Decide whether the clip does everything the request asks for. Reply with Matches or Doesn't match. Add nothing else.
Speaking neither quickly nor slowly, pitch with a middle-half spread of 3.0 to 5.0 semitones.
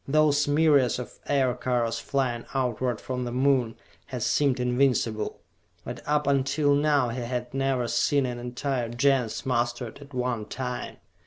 Doesn't match